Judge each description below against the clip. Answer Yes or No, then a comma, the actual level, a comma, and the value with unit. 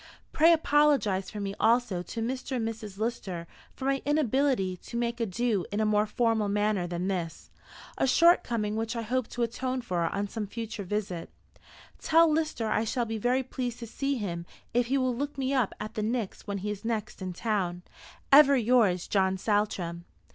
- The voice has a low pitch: No, high, 225 Hz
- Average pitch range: Yes, average, 4.0 semitones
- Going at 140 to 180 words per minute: No, average, 190 wpm